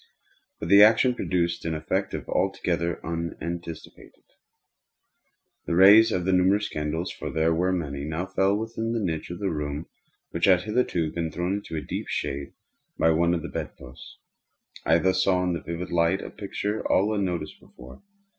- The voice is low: Yes, very low, 85 Hz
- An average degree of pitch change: Yes, average, 3.0 semitones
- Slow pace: No, average, 165 wpm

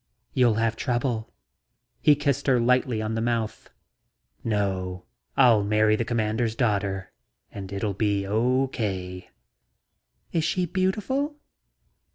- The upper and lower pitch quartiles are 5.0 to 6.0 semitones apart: No, average, 3.8 semitones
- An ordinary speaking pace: No, slow, 120 wpm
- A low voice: Yes, low, 115 Hz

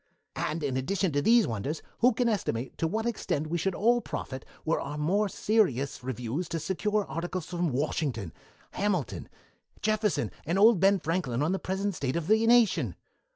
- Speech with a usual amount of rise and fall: No, wide, 6.4 semitones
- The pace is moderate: Yes, average, 175 wpm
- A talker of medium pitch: Yes, medium, 175 Hz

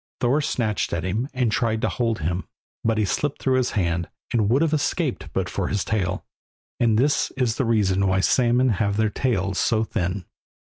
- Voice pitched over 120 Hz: No, low, 110 Hz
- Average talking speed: Yes, average, 195 wpm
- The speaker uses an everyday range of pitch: Yes, average, 4.6 semitones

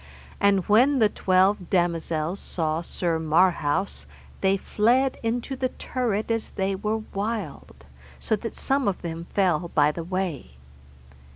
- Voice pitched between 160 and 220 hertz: Yes, high, 190 Hz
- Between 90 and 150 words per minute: Yes, slow, 135 wpm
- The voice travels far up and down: No, average, 4.6 semitones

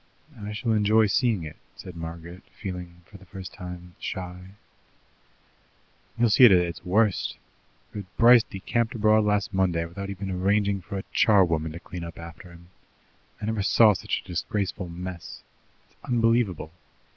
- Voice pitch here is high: No, very low, 95 Hz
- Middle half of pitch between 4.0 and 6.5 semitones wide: No, average, 3.3 semitones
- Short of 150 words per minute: No, average, 155 wpm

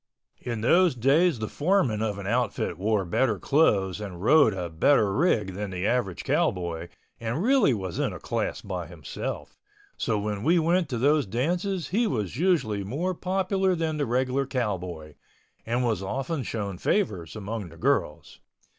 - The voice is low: Yes, low, 115 Hz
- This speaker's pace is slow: No, average, 165 wpm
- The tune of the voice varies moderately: No, wide, 8.1 semitones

